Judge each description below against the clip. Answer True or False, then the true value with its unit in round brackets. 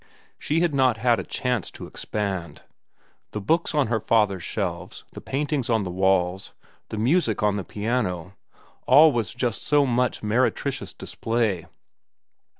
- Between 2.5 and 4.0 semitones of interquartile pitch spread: False (4.8 semitones)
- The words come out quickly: False (145 wpm)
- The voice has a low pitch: True (115 Hz)